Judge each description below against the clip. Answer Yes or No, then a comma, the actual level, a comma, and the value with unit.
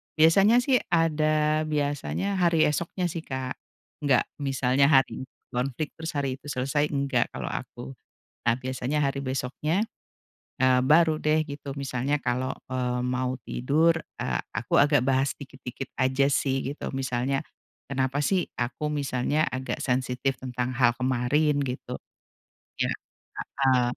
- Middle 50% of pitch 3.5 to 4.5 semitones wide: No, average, 2.9 semitones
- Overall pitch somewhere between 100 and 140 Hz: Yes, low, 135 Hz